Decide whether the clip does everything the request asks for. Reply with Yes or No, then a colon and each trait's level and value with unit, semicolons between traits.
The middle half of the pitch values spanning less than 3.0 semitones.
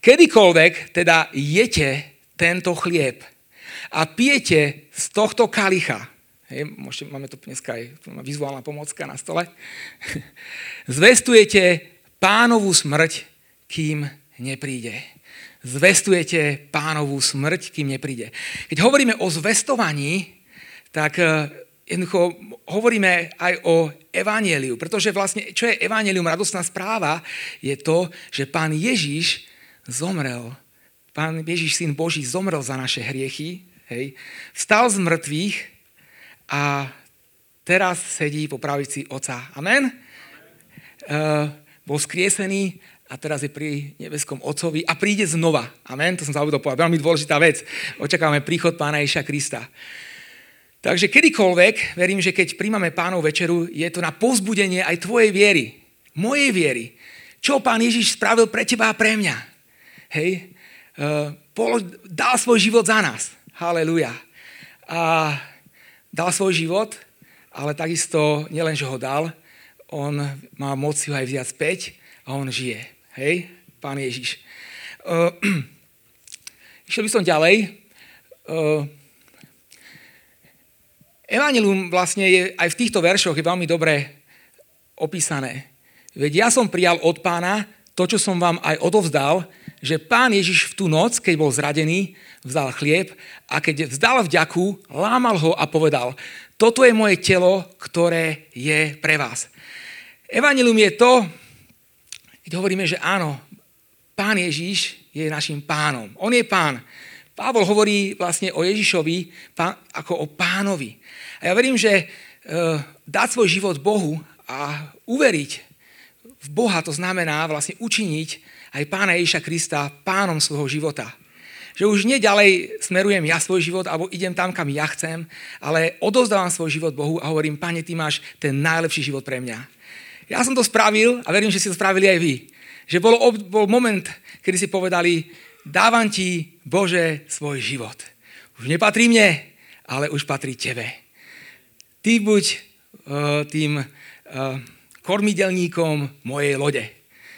No: average, 4.8 semitones